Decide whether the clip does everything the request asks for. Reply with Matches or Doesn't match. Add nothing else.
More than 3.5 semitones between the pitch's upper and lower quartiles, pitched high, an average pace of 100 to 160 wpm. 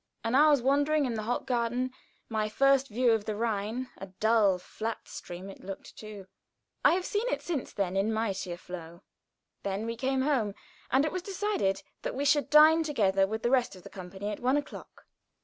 Doesn't match